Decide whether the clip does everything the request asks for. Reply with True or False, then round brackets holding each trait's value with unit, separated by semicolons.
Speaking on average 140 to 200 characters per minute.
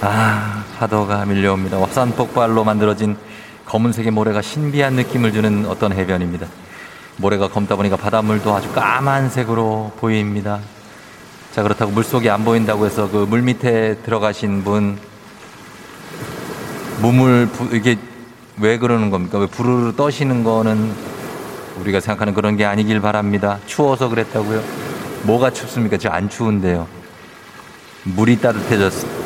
False (310 characters per minute)